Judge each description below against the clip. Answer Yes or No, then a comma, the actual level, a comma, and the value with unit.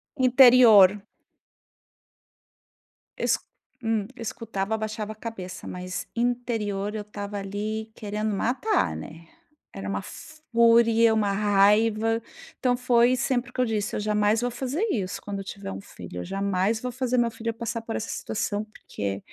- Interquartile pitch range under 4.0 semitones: Yes, average, 2.8 semitones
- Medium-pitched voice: No, high, 215 Hz